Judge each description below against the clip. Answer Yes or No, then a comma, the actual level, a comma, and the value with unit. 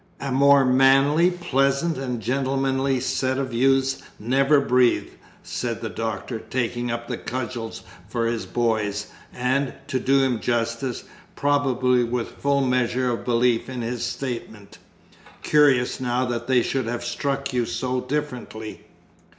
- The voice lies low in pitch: Yes, low, 125 Hz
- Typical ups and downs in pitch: No, narrow, 2.3 semitones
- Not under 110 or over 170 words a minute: Yes, average, 140 wpm